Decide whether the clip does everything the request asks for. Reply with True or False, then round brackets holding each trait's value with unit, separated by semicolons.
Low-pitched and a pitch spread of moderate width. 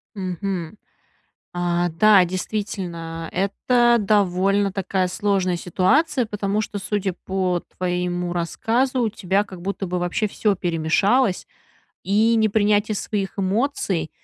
False (195 Hz; 3.0 semitones)